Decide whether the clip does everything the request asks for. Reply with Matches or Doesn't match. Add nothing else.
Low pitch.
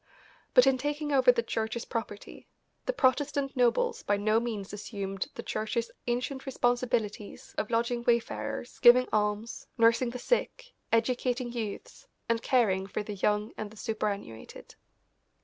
Doesn't match